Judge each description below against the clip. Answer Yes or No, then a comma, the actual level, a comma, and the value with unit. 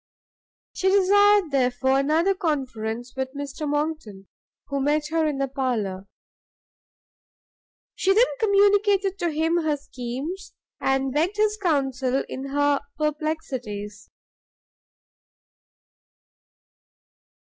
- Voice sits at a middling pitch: No, very high, 290 Hz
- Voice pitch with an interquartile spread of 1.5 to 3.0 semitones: No, average, 4.8 semitones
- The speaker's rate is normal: No, slow, 95 wpm